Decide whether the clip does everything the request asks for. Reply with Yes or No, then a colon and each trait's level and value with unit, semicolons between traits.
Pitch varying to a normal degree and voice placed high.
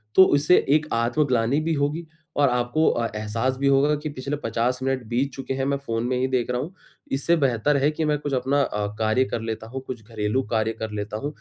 No: average, 3.8 semitones; low, 130 Hz